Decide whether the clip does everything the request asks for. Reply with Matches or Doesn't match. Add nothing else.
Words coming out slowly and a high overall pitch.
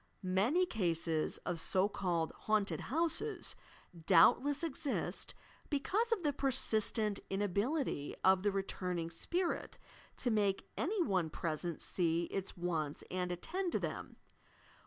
Matches